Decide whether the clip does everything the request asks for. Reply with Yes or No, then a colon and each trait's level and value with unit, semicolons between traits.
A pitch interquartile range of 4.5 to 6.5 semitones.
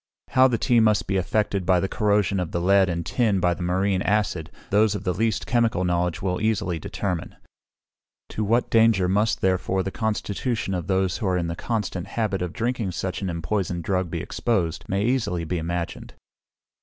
No: average, 3.2 semitones